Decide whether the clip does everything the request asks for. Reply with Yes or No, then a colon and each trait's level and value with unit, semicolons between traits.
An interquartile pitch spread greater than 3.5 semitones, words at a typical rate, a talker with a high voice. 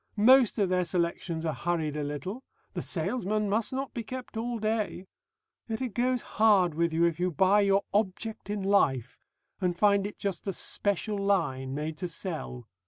Yes: average, 4.2 semitones; average, 180 wpm; high, 195 Hz